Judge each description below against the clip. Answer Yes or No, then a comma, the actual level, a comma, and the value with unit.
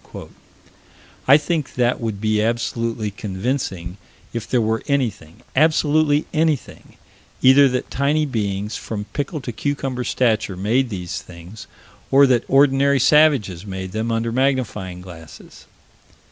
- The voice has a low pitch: Yes, low, 120 Hz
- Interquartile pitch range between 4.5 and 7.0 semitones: Yes, average, 5.2 semitones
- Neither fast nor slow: No, slow, 125 wpm